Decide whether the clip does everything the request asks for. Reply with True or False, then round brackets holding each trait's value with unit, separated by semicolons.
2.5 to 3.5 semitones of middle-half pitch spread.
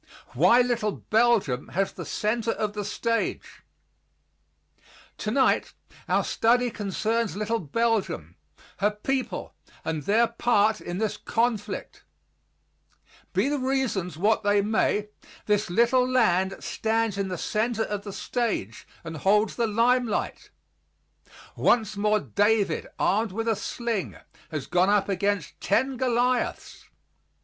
True (2.9 semitones)